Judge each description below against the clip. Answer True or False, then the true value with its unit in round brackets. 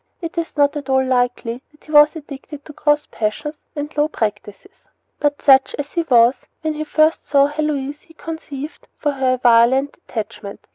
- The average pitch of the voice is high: True (285 Hz)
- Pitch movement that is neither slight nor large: True (3.0 semitones)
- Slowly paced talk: False (185 wpm)